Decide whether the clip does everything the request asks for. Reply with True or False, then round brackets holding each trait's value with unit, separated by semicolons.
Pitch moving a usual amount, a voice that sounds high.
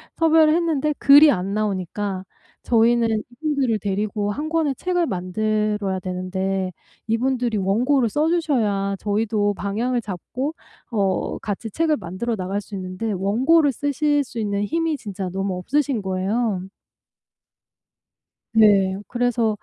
False (5.7 semitones; 215 Hz)